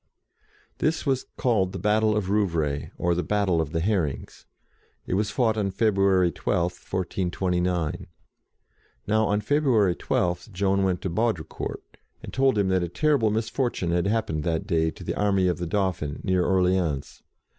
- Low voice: Yes, very low, 95 Hz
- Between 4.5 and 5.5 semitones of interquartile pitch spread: No, average, 3.5 semitones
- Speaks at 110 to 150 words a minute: No, average, 160 wpm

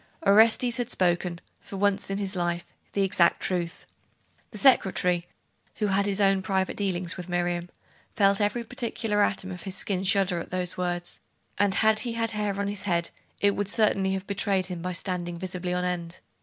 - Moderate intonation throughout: No, narrow, 2.3 semitones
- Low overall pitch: No, high, 190 Hz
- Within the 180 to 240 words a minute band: Yes, average, 190 wpm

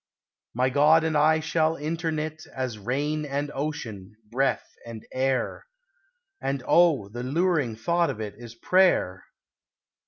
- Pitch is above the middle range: No, medium, 145 Hz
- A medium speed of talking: No, slow, 130 wpm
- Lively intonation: No, average, 4.7 semitones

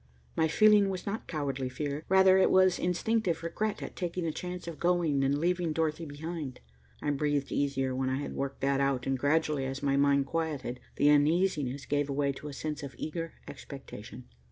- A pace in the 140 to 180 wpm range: No, average, 190 wpm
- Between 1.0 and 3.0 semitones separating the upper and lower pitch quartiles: No, average, 3.8 semitones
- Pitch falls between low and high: Yes, medium, 150 Hz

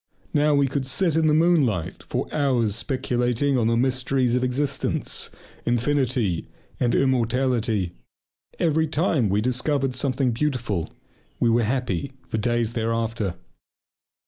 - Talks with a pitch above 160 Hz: No, low, 125 Hz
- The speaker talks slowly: Yes, slow, 125 wpm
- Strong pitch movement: No, average, 3.3 semitones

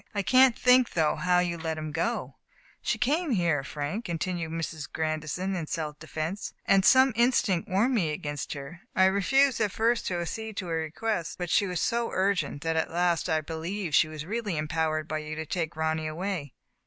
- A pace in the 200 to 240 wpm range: Yes, fast, 205 wpm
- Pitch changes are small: No, average, 4.6 semitones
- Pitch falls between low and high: Yes, medium, 170 Hz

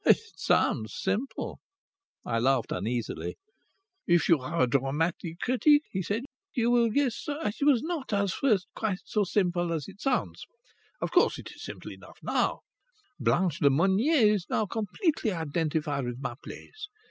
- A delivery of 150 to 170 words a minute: Yes, average, 160 wpm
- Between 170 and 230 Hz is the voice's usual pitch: Yes, high, 190 Hz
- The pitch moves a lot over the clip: Yes, wide, 8.0 semitones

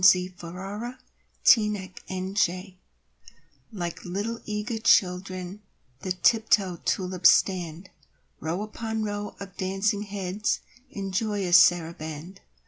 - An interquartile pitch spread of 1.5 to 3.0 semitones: Yes, narrow, 2.5 semitones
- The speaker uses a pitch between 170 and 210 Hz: Yes, high, 190 Hz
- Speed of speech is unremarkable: No, slow, 95 wpm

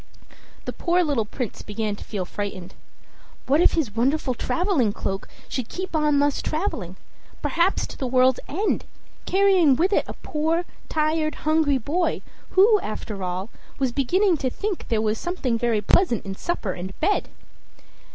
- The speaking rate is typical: Yes, average, 160 wpm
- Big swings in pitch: Yes, wide, 7.8 semitones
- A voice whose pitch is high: Yes, very high, 280 Hz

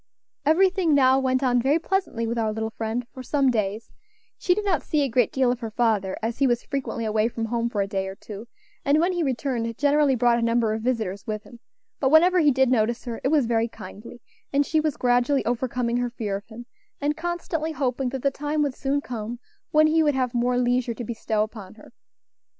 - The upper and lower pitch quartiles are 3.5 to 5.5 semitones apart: Yes, average, 4.0 semitones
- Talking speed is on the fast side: Yes, fast, 225 wpm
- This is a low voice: No, high, 245 Hz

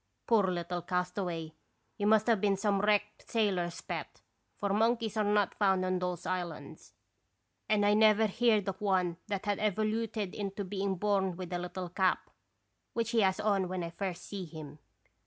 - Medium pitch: No, high, 195 Hz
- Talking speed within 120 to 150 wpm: No, average, 175 wpm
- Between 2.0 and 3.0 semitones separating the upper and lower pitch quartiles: Yes, narrow, 2.6 semitones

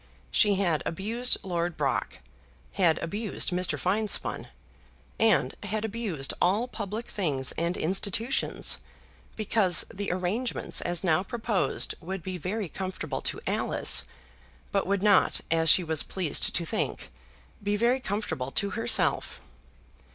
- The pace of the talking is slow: Yes, slow, 130 wpm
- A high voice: Yes, high, 195 Hz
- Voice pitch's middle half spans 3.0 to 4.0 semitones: Yes, average, 3.7 semitones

